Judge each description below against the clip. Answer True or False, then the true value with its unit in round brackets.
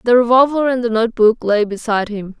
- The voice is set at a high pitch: True (230 Hz)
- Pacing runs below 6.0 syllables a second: False (6.2 syllables/s)